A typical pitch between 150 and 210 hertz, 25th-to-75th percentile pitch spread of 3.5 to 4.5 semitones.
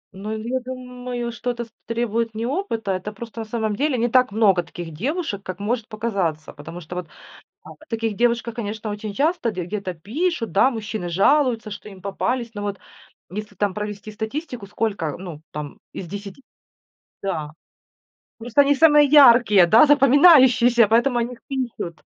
No: high, 225 Hz; average, 3.8 semitones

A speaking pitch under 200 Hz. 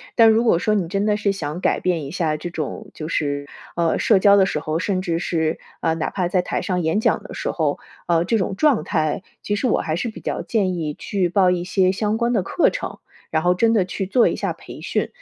Yes: medium, 185 Hz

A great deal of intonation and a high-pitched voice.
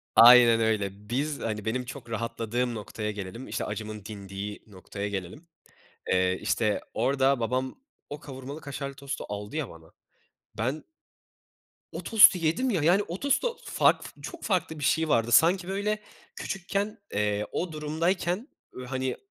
No: wide, 7.2 semitones; low, 130 Hz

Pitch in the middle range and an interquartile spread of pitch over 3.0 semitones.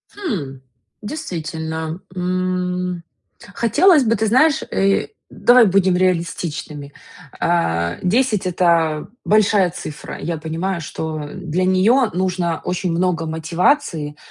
Yes: medium, 180 Hz; average, 3.7 semitones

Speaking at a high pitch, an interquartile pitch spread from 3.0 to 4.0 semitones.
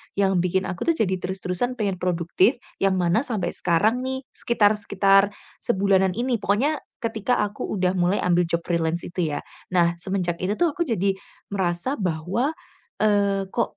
Yes: high, 195 Hz; average, 3.6 semitones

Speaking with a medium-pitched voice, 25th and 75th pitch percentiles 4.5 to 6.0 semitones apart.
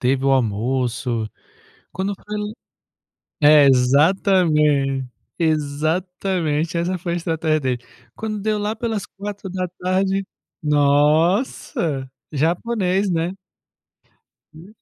Yes: medium, 165 Hz; average, 5.1 semitones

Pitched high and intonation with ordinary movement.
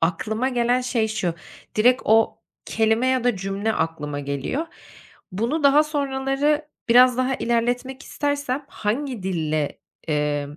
No: high, 235 Hz; wide, 5.8 semitones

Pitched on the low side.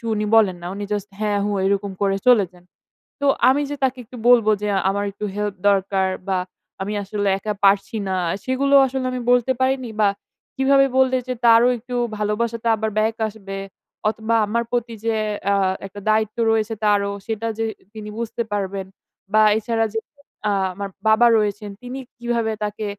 No: high, 220 Hz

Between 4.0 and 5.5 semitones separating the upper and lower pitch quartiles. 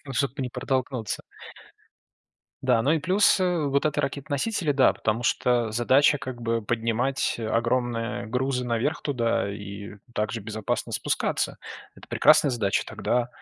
No: average, 3.4 semitones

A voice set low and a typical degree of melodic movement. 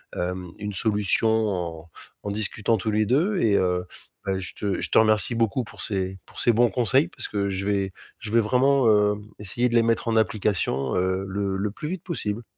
Yes: low, 105 Hz; average, 3.1 semitones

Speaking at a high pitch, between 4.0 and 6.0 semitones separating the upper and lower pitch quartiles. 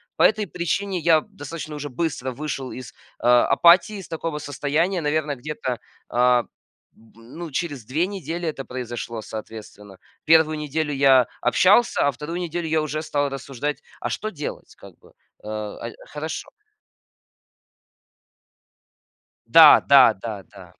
No: medium, 150 Hz; average, 4.6 semitones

